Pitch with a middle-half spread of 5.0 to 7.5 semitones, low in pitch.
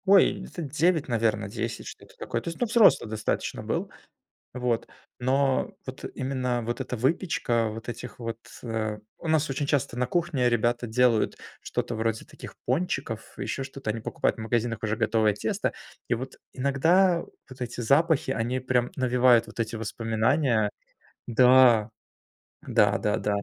No: average, 3.3 semitones; low, 125 Hz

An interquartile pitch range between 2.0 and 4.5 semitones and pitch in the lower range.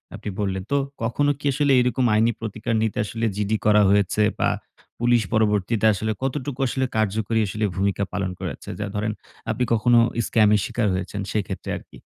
Yes: average, 2.7 semitones; low, 110 Hz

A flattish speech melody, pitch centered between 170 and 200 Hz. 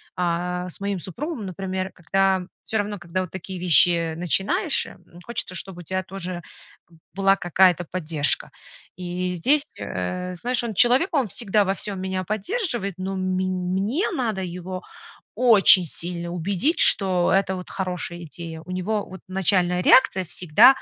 Yes: narrow, 2.2 semitones; medium, 185 Hz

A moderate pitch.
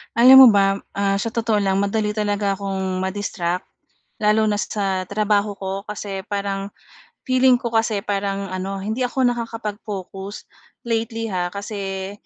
No: high, 205 Hz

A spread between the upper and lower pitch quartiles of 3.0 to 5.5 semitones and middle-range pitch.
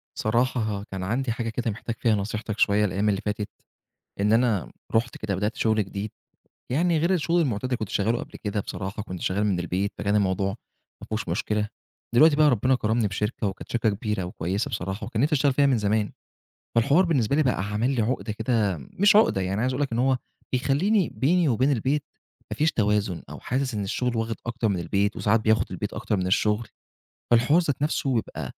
No: average, 4.2 semitones; low, 110 Hz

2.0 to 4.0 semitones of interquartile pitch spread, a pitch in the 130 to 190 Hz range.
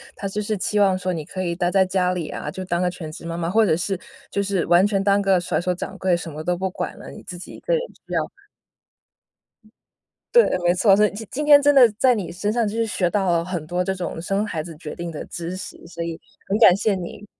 Yes: average, 2.9 semitones; medium, 185 Hz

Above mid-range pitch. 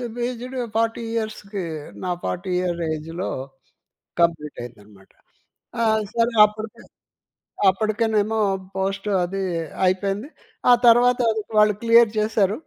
Yes: high, 210 Hz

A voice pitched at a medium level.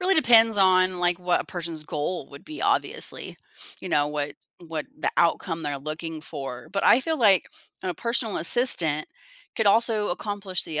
Yes: medium, 180 Hz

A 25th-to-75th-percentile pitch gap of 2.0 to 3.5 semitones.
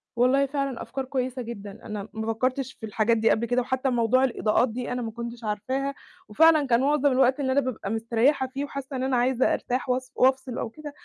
Yes: narrow, 2.5 semitones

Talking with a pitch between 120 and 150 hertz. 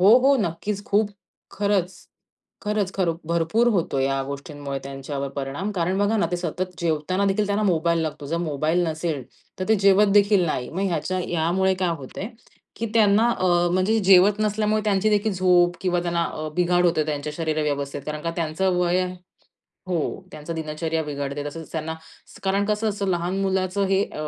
No: medium, 180 Hz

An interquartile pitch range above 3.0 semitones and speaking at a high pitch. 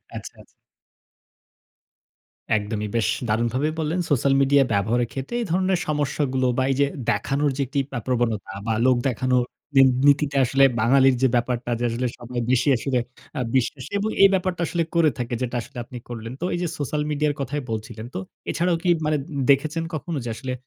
No: average, 3.7 semitones; low, 135 Hz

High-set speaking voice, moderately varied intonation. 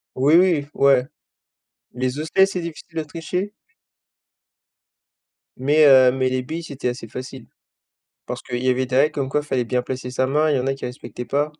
No: low, 135 Hz; average, 3.1 semitones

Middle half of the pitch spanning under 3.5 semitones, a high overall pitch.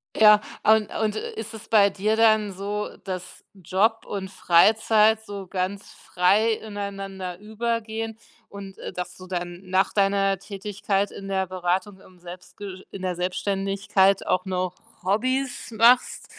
Yes: narrow, 2.4 semitones; high, 195 Hz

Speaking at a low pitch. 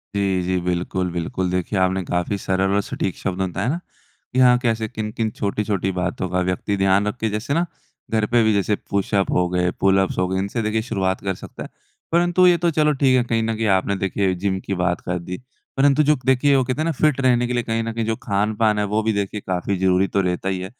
Yes: low, 100 Hz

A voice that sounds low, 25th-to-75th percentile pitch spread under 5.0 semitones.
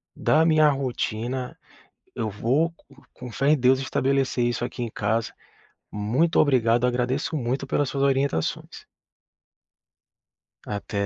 Yes: low, 125 Hz; average, 2.9 semitones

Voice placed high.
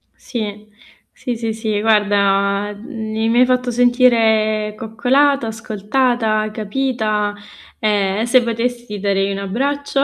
Yes: high, 220 Hz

